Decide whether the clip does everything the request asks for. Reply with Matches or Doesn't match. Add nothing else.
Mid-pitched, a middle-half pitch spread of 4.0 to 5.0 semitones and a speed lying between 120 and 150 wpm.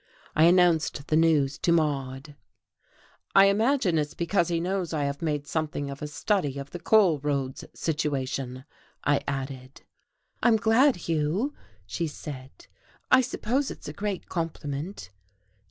Matches